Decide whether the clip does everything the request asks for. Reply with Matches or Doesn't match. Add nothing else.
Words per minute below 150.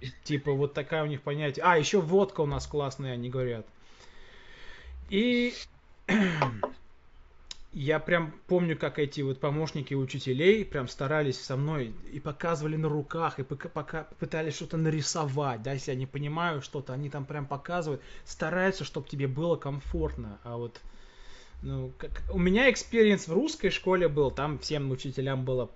Doesn't match